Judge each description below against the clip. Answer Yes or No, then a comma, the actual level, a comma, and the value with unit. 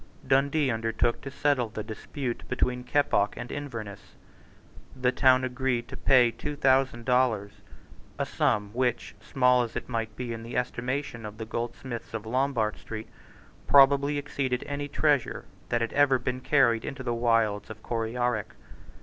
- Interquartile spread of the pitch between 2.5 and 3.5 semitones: Yes, average, 2.8 semitones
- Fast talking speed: No, average, 155 wpm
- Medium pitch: No, low, 125 Hz